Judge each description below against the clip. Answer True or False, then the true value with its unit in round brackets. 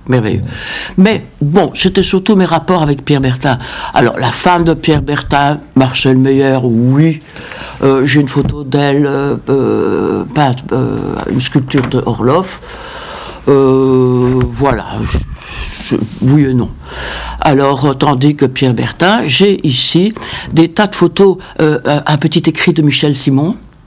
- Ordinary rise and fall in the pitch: True (3.7 semitones)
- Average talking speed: False (140 wpm)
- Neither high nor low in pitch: True (145 Hz)